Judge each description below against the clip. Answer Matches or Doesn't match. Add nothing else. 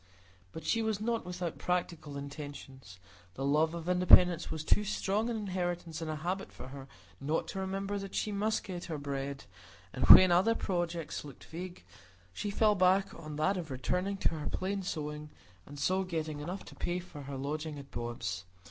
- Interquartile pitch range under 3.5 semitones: Doesn't match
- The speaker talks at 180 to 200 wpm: Matches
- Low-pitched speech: Doesn't match